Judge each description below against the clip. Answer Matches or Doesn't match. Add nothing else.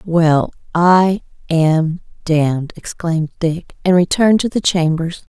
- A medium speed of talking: Doesn't match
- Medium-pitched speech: Matches